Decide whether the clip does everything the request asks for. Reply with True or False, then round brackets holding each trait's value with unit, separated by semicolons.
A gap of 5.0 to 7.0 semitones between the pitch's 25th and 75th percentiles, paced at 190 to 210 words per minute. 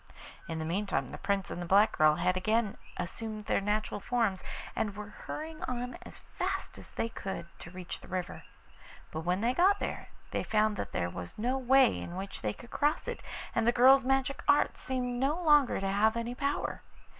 True (5.5 semitones; 200 wpm)